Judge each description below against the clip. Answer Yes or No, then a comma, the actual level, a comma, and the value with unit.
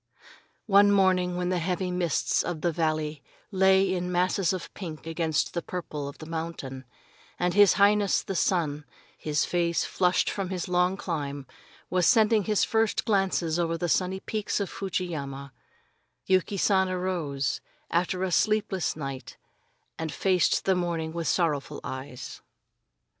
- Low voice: No, medium, 180 Hz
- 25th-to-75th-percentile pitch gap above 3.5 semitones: No, average, 3.1 semitones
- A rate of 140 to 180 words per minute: Yes, average, 155 wpm